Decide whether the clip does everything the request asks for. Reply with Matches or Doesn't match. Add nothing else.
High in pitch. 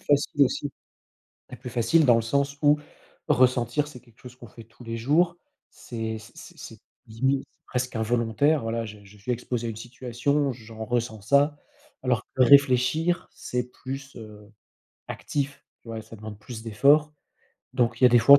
Doesn't match